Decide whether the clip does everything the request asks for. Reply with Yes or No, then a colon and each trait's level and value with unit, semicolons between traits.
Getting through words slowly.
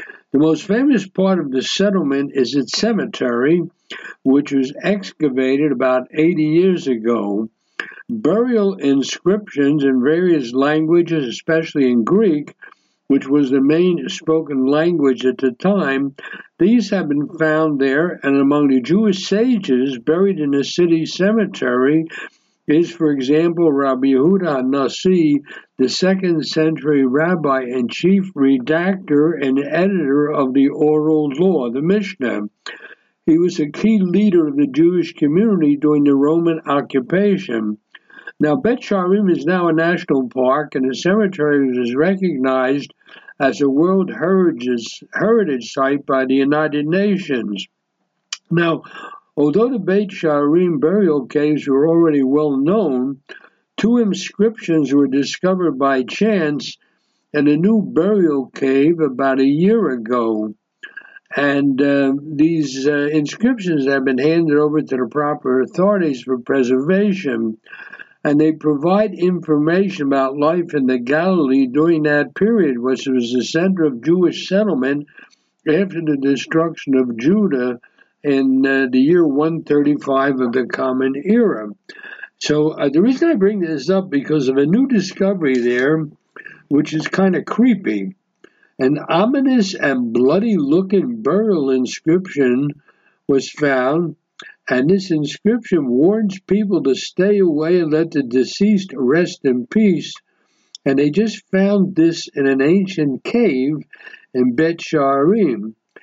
Yes: slow, 130 wpm